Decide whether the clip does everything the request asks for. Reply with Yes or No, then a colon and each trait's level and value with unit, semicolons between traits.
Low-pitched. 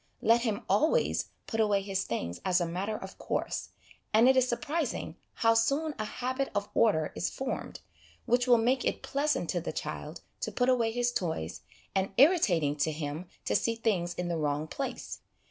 No: high, 225 Hz